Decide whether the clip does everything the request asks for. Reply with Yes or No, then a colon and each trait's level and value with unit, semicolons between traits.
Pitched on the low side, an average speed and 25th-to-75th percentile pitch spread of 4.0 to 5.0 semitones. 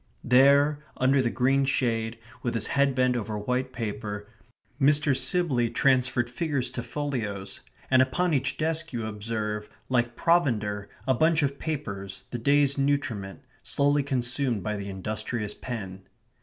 Yes: low, 125 Hz; average, 145 wpm; average, 4.5 semitones